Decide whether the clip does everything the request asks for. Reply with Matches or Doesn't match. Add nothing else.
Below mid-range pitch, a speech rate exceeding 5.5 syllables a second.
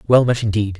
Matches